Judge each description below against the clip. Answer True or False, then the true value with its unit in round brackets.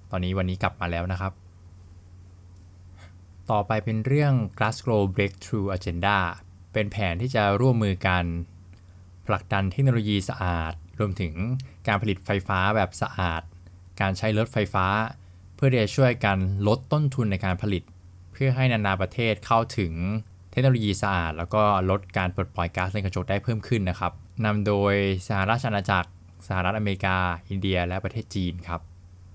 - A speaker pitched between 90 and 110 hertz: True (95 Hz)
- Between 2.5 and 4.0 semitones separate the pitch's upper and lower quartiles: True (3.0 semitones)